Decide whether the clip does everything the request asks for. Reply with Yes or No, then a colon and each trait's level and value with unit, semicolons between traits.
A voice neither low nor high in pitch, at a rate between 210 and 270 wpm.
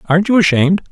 No: medium, 180 Hz; average, 200 wpm